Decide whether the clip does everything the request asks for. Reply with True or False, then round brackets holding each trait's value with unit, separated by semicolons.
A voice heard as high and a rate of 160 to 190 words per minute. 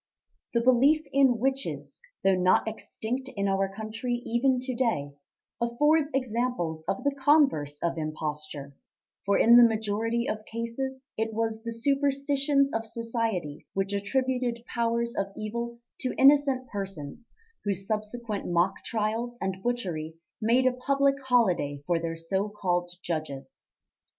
False (230 Hz; 135 wpm)